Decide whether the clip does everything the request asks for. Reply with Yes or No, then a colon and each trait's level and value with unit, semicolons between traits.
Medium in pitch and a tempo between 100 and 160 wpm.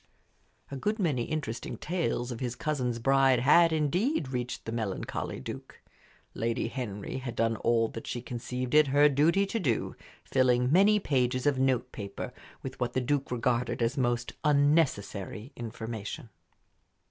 No: low, 130 Hz; average, 150 wpm